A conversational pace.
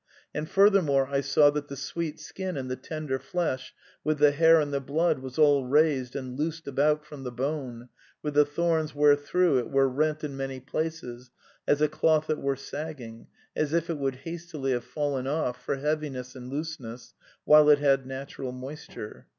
Yes: average, 190 wpm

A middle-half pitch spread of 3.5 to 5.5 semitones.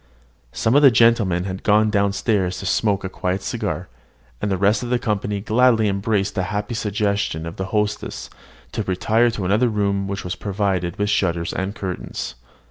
No: narrow, 2.4 semitones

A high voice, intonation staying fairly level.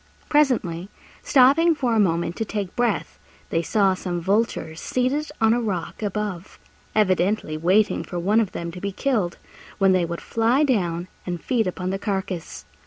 No: high, 200 Hz; average, 4.5 semitones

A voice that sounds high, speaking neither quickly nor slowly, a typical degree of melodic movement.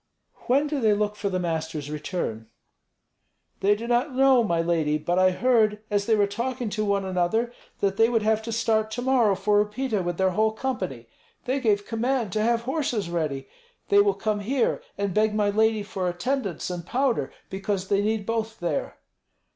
Yes: high, 210 Hz; average, 190 wpm; average, 4.0 semitones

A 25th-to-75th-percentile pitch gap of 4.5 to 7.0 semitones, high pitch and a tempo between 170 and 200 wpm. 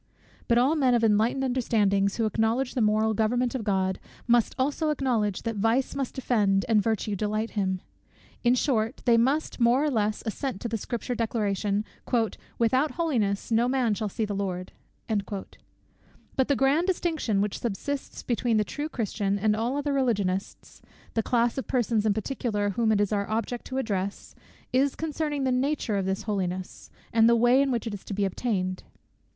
No: average, 3.9 semitones; high, 225 Hz; average, 180 wpm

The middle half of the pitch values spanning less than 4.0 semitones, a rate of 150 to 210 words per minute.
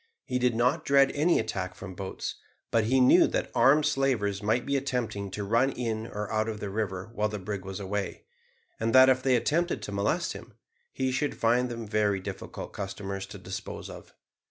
No: average, 4.3 semitones; average, 200 wpm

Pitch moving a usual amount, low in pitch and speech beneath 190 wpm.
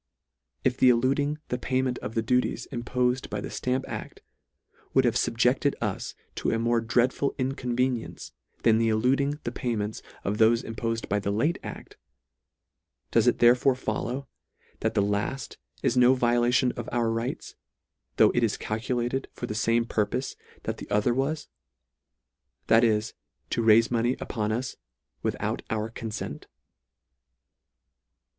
No: narrow, 2.3 semitones; low, 120 Hz; average, 150 wpm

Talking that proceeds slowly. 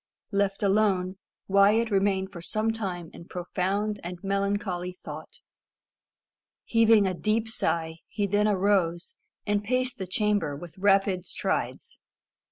Yes: slow, 125 wpm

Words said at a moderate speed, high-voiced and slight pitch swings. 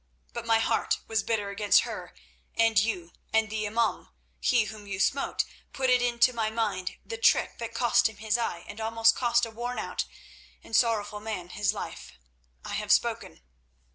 Yes: average, 175 wpm; high, 225 Hz; narrow, 2.1 semitones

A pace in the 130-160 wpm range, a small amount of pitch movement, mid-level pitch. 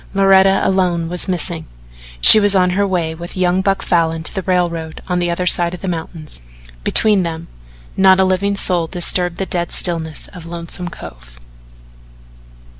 No: average, 170 wpm; narrow, 2.2 semitones; medium, 180 Hz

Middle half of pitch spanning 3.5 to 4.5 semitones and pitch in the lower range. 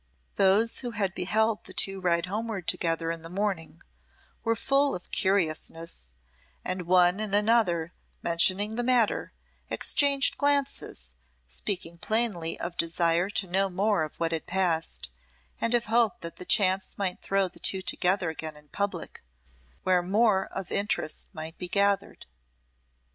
No: average, 3.8 semitones; high, 190 Hz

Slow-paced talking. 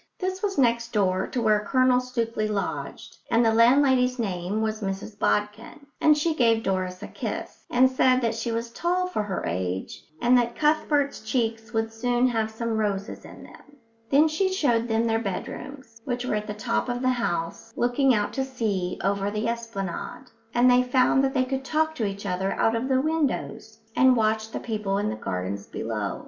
No: average, 195 wpm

